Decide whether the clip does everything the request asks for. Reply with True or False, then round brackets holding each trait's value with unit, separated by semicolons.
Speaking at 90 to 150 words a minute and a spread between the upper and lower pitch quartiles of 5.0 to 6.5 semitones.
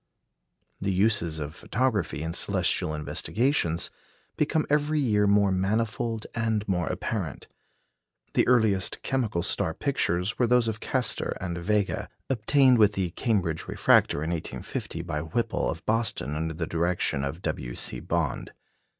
True (140 wpm; 5.4 semitones)